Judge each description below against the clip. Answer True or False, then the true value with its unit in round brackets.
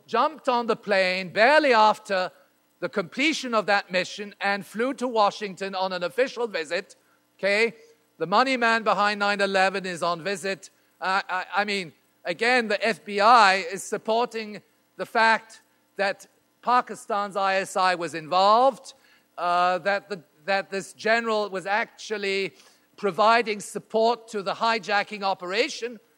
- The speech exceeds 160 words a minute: False (135 wpm)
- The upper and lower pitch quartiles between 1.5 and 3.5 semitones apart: True (3.1 semitones)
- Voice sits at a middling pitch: False (205 Hz)